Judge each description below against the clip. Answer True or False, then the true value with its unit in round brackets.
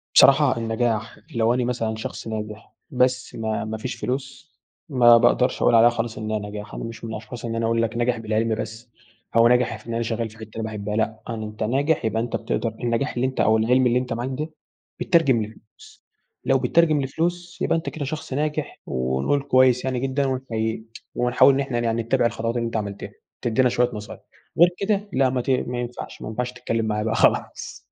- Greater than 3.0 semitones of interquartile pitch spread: False (2.6 semitones)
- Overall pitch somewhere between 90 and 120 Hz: True (115 Hz)